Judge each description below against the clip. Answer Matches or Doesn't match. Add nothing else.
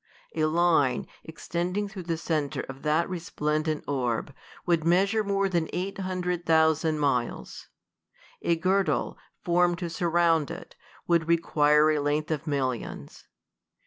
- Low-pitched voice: Doesn't match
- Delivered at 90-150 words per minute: Matches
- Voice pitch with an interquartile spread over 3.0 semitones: Doesn't match